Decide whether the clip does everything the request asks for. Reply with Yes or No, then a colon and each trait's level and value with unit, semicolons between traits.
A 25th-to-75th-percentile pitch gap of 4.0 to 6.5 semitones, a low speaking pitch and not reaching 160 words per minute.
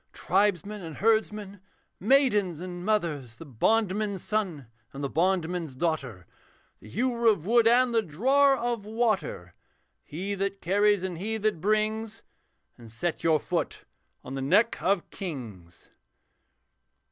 No: average, 5.2 semitones; high, 195 Hz; slow, 135 wpm